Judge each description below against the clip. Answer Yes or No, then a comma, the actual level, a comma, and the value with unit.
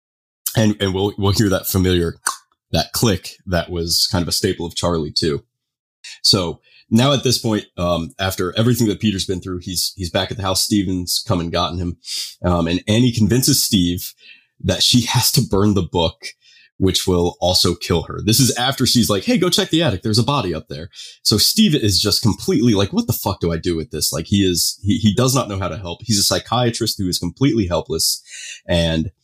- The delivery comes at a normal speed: No, fast, 220 wpm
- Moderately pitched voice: No, low, 100 Hz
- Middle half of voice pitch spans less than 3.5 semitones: No, average, 4.8 semitones